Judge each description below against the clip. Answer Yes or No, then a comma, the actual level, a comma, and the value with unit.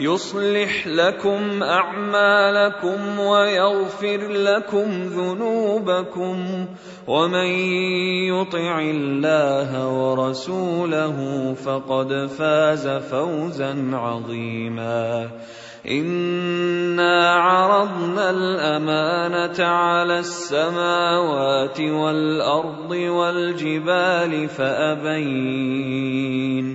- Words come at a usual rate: No, slow, 50 wpm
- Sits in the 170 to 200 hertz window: Yes, medium, 175 Hz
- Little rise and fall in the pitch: No, average, 4.9 semitones